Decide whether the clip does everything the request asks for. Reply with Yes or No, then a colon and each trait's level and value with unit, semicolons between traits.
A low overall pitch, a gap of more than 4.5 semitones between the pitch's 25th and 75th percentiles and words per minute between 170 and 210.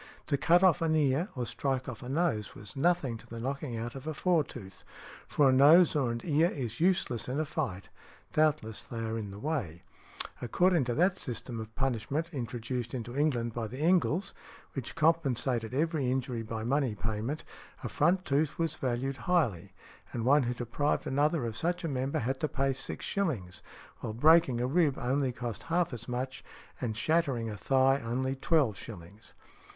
Yes: low, 130 Hz; average, 4.9 semitones; average, 185 wpm